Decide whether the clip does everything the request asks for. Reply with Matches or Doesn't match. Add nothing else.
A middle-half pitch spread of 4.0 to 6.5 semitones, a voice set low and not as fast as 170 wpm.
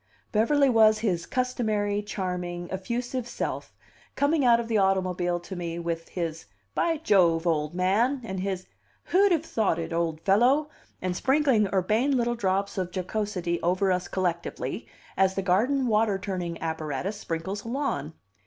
Doesn't match